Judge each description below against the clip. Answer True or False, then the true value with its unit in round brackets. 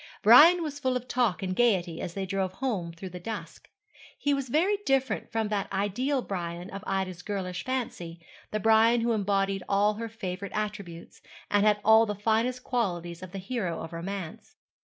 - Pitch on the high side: True (205 Hz)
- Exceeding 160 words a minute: True (180 wpm)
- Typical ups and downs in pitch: True (4.4 semitones)